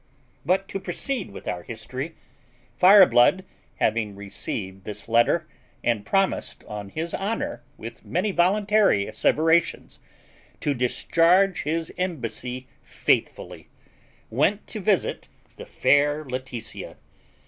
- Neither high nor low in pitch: Yes, medium, 145 Hz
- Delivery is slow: Yes, slow, 105 wpm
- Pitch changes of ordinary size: No, wide, 8.0 semitones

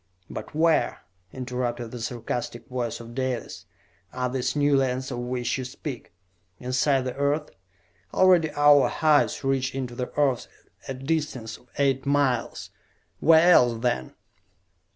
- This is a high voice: No, low, 130 Hz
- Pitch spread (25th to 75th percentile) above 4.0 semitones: No, narrow, 2.6 semitones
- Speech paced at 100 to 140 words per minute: Yes, slow, 135 wpm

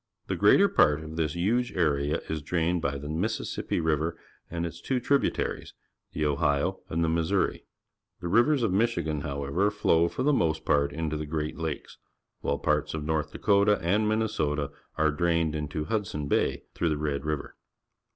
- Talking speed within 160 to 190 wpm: Yes, average, 170 wpm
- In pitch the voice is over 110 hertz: No, very low, 80 Hz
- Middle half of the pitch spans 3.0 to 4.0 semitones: Yes, average, 3.6 semitones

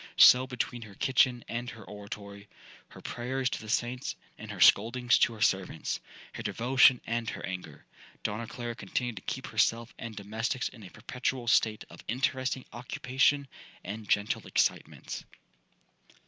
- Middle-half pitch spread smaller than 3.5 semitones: Yes, average, 2.7 semitones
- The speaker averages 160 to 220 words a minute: No, average, 140 wpm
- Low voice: Yes, low, 120 Hz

